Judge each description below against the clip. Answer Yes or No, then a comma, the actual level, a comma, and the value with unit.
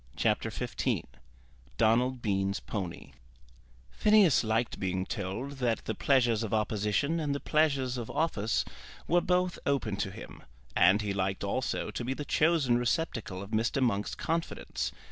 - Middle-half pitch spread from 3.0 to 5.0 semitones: No, wide, 5.6 semitones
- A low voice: Yes, low, 120 Hz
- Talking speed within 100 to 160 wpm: Yes, average, 145 wpm